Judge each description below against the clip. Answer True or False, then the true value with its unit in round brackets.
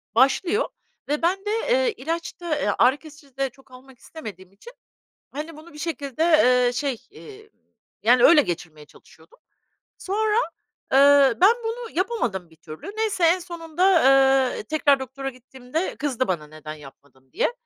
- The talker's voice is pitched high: True (280 Hz)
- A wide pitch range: True (5.7 semitones)